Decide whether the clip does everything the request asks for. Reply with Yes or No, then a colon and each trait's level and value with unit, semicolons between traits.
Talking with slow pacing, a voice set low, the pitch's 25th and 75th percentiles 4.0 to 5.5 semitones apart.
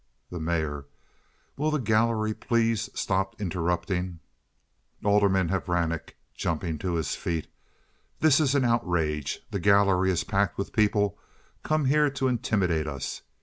Yes: slow, 130 wpm; very low, 95 Hz; average, 5.1 semitones